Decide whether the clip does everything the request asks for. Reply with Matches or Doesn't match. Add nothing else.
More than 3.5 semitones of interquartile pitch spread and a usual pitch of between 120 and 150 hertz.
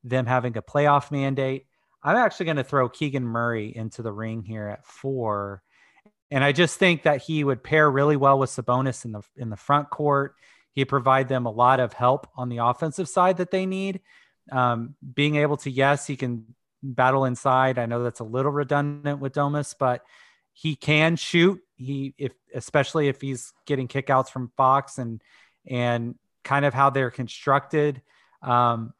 Doesn't match